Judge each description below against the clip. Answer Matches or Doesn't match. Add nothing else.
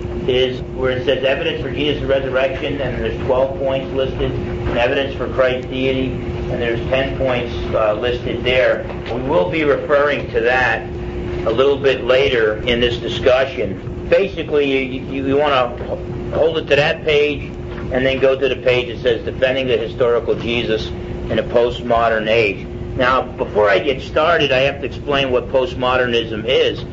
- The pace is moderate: Matches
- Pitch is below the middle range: Matches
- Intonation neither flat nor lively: Doesn't match